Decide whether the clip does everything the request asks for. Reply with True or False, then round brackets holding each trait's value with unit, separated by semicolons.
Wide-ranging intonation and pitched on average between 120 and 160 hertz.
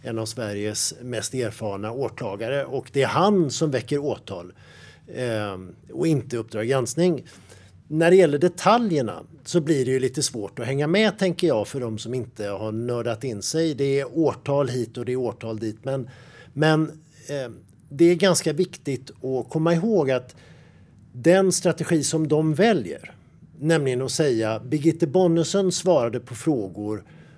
True (5.7 semitones; 135 Hz)